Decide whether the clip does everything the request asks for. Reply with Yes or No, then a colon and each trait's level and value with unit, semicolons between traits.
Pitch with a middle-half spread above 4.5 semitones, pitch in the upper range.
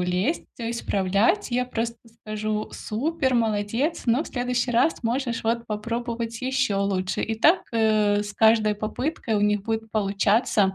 No: average, 2.8 semitones; high, 225 Hz